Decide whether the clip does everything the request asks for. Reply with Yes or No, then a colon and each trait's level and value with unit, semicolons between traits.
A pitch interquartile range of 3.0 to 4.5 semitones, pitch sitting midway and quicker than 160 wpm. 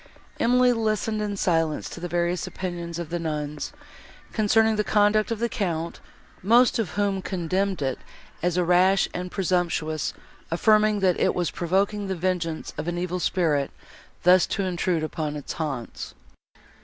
No: average, 3.7 semitones; medium, 180 Hz; average, 155 wpm